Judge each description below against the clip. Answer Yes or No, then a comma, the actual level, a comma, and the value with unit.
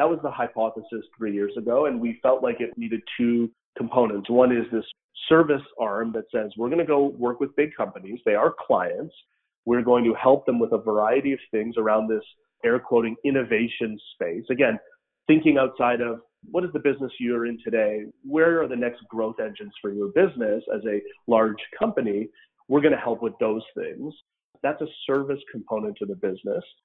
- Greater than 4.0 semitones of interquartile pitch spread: Yes, average, 4.7 semitones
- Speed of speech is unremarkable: Yes, average, 190 wpm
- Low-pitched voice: Yes, low, 120 Hz